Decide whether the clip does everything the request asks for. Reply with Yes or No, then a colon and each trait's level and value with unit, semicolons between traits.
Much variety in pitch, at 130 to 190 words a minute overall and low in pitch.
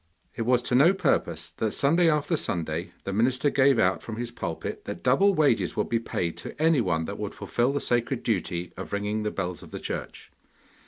No: wide, 6.6 semitones; fast, 205 wpm; low, 120 Hz